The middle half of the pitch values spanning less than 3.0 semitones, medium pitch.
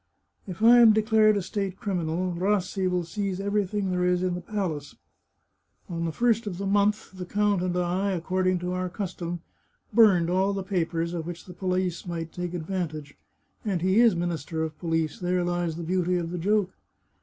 Yes: narrow, 2.4 semitones; medium, 180 Hz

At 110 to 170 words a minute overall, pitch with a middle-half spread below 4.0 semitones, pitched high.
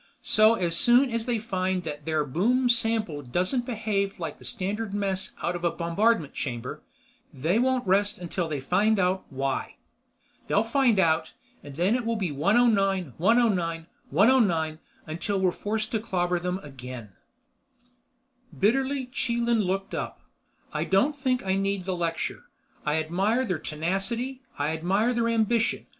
No: average, 150 wpm; wide, 5.5 semitones; high, 195 Hz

